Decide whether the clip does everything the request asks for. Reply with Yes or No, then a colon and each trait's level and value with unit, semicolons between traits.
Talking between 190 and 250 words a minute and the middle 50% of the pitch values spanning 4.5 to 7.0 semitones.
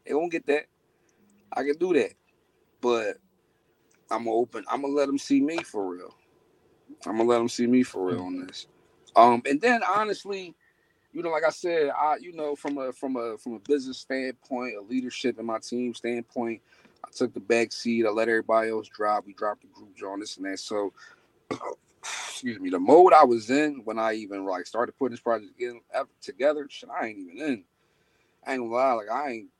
Yes: fast, 205 wpm; average, 4.8 semitones